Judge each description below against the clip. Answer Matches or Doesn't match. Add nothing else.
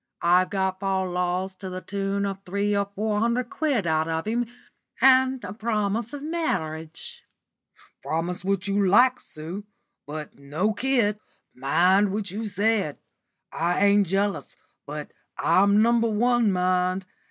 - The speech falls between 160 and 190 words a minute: Doesn't match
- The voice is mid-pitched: Doesn't match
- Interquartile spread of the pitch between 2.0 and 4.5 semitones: Matches